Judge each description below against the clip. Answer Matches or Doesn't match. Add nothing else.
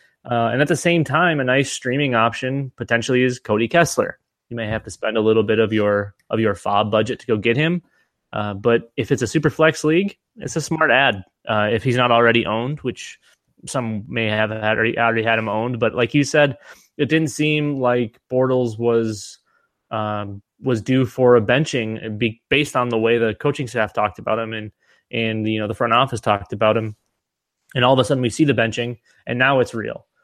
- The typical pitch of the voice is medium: Doesn't match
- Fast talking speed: Matches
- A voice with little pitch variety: Doesn't match